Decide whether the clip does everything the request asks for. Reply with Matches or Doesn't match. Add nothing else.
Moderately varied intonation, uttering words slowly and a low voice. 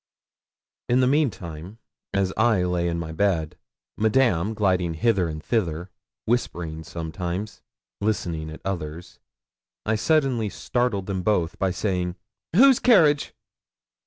Matches